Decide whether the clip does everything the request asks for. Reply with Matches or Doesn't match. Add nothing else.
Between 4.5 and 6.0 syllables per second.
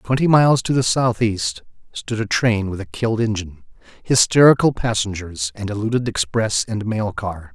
Matches